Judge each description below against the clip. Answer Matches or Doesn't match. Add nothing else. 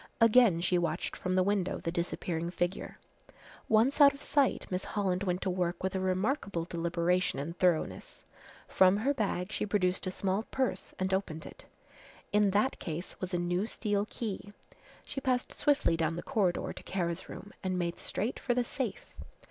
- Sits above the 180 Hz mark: Matches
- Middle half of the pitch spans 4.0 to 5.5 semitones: Doesn't match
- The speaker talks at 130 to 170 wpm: Doesn't match